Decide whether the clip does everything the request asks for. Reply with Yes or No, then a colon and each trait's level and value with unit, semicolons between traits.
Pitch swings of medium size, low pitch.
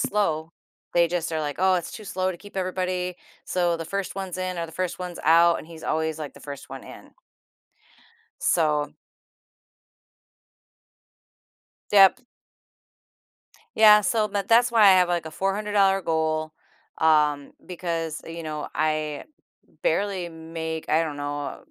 No: average, 3.1 semitones; medium, 170 Hz